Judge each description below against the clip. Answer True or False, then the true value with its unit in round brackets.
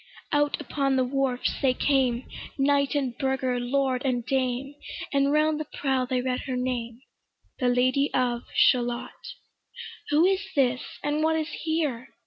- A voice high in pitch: True (265 Hz)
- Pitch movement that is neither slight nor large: False (2.3 semitones)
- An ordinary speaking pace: True (150 wpm)